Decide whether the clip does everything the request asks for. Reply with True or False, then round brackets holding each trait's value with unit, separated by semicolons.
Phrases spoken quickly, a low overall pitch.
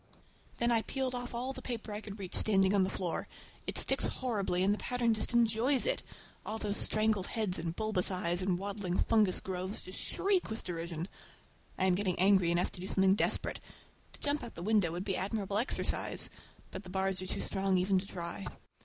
False (210 wpm; 195 Hz)